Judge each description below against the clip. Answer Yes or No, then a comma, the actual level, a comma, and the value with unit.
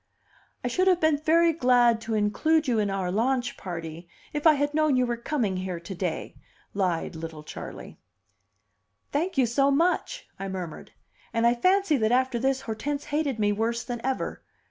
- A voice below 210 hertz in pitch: No, high, 245 Hz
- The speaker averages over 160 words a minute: Yes, average, 180 wpm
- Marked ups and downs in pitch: Yes, wide, 6.3 semitones